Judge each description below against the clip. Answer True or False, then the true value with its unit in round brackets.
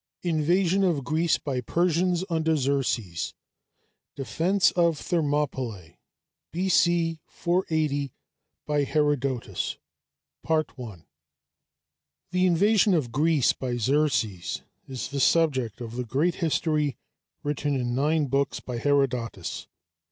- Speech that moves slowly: True (95 wpm)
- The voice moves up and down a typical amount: True (4.6 semitones)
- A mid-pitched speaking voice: True (145 Hz)